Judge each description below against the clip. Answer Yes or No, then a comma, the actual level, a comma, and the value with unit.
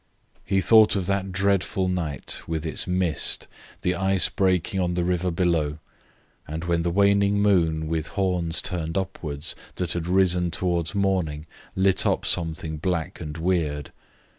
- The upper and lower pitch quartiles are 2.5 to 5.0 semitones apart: Yes, average, 2.8 semitones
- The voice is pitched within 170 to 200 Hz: No, very low, 90 Hz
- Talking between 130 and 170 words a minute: Yes, average, 150 wpm